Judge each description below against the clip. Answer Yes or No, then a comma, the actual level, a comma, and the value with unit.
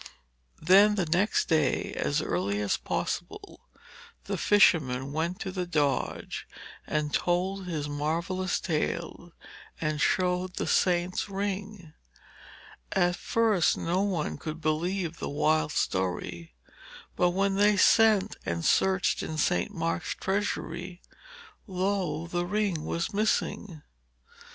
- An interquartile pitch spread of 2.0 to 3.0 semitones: No, average, 3.8 semitones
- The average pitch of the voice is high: No, medium, 175 Hz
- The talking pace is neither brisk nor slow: No, slow, 115 wpm